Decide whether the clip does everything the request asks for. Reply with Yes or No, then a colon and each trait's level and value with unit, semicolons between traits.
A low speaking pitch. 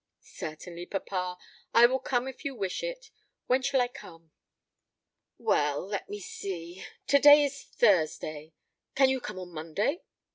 No: high, 200 Hz